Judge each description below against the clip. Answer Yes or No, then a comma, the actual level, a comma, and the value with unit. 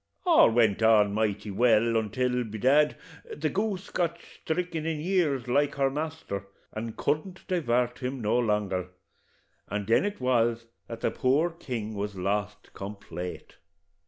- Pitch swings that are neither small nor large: No, wide, 6.4 semitones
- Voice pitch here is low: Yes, low, 120 Hz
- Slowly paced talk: No, average, 145 wpm